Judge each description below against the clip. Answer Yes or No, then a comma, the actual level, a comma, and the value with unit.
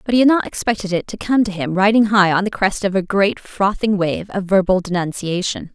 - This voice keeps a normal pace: No, fast, 240 wpm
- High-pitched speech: Yes, high, 195 Hz